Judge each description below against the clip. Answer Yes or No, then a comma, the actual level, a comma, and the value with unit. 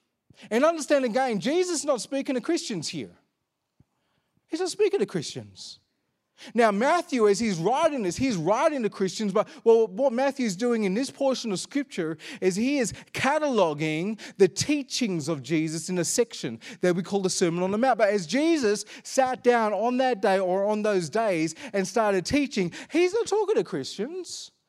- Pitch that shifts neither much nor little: No, wide, 6.6 semitones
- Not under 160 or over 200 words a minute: Yes, average, 180 wpm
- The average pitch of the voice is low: No, high, 225 Hz